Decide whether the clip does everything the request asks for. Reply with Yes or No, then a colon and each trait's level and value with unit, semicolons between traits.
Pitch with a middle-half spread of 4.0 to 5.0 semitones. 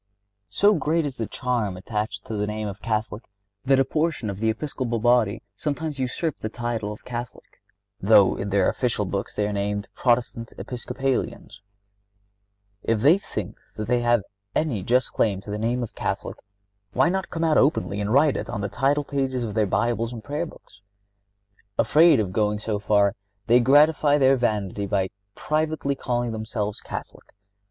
Yes: average, 4.4 semitones